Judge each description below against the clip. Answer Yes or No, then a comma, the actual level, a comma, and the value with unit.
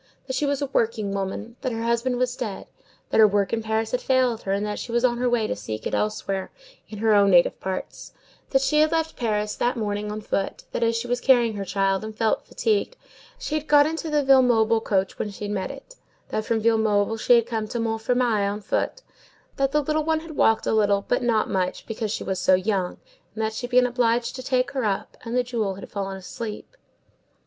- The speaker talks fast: Yes, fast, 235 wpm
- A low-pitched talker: No, high, 225 Hz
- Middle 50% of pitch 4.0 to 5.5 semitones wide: No, average, 3.3 semitones